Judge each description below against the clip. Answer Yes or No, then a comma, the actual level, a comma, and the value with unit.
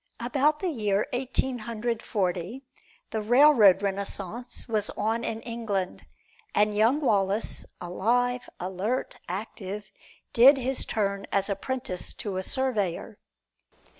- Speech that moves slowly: Yes, slow, 115 wpm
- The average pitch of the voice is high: Yes, high, 220 Hz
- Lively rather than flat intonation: No, average, 3.9 semitones